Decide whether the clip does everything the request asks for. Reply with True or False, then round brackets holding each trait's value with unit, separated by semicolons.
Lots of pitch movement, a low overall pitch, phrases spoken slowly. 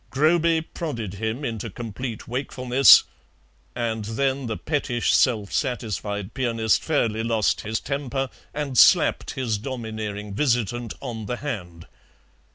False (3.6 semitones; 120 Hz; 120 wpm)